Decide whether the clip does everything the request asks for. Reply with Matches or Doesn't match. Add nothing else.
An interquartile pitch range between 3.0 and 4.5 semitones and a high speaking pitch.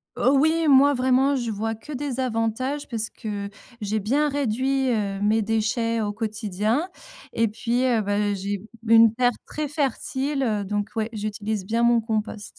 Matches